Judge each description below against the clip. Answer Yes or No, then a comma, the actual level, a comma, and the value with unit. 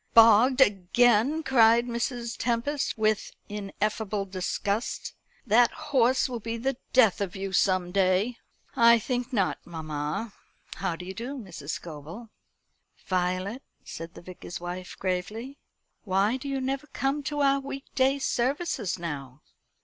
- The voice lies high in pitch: Yes, high, 225 Hz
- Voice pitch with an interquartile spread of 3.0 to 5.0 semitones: No, wide, 5.5 semitones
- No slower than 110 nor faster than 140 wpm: Yes, slow, 135 wpm